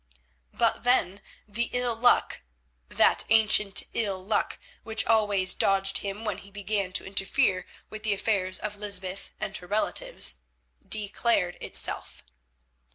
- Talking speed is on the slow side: Yes, slow, 120 wpm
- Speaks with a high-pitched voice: Yes, high, 200 Hz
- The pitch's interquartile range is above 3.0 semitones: No, average, 2.7 semitones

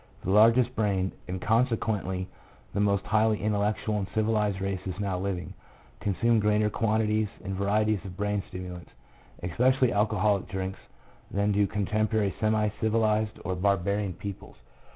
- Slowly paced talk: Yes, slow, 130 wpm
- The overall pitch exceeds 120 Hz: No, low, 105 Hz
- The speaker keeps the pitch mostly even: Yes, narrow, 2.0 semitones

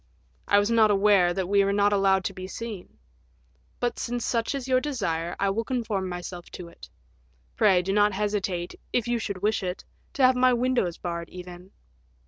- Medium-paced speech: Yes, average, 190 wpm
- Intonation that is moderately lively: Yes, average, 4.2 semitones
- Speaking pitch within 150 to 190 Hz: No, high, 200 Hz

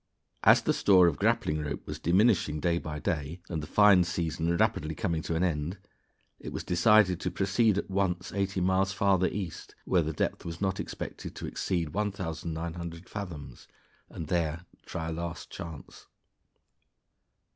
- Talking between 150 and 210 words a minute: Yes, average, 160 wpm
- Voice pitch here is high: No, very low, 85 Hz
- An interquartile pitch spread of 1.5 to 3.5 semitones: Yes, average, 3.0 semitones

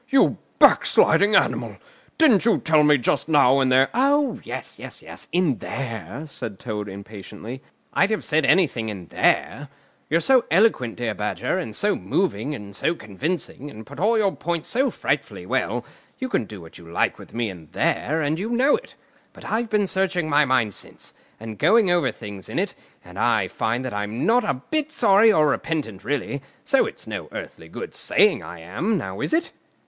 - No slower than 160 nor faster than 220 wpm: Yes, average, 185 wpm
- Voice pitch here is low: No, medium, 145 Hz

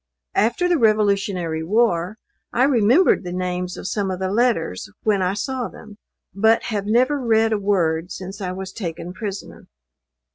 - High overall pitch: Yes, high, 200 Hz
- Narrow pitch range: No, average, 3.7 semitones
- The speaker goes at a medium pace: Yes, average, 160 wpm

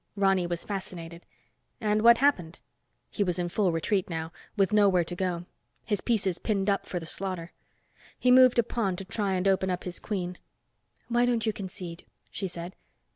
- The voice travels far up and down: No, average, 3.1 semitones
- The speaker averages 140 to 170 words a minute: No, average, 185 wpm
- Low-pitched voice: No, high, 190 Hz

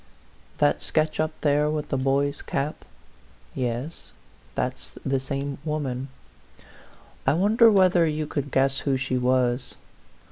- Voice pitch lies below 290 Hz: Yes, medium, 140 Hz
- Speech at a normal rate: No, slow, 130 wpm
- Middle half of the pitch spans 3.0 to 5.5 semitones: No, narrow, 2.6 semitones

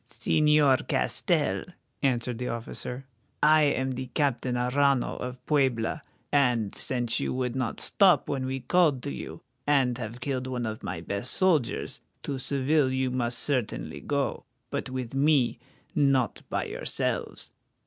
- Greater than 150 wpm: No, average, 145 wpm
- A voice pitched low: Yes, low, 130 Hz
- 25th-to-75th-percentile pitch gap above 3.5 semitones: No, narrow, 2.5 semitones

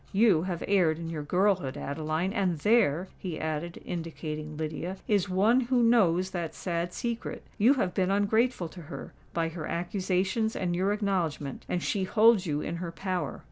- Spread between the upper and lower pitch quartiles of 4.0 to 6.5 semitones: No, average, 3.6 semitones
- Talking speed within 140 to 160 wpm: No, average, 170 wpm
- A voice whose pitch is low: No, medium, 180 Hz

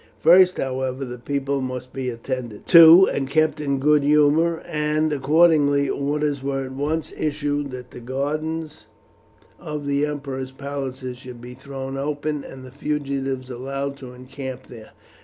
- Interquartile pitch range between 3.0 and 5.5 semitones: No, narrow, 2.4 semitones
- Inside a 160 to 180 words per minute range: No, average, 150 wpm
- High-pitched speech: No, medium, 140 Hz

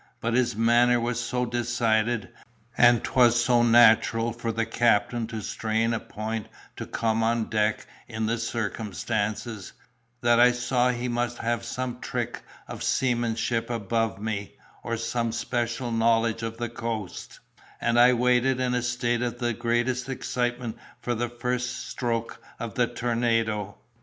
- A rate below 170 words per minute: Yes, average, 150 wpm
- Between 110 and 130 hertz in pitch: Yes, low, 120 Hz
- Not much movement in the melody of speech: Yes, narrow, 1.2 semitones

